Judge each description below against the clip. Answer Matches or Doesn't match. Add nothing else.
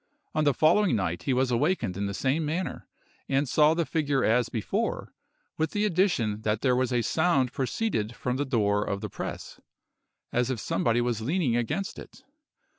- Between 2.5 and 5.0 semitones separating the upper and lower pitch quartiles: Doesn't match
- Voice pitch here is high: Doesn't match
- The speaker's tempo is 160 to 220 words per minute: Matches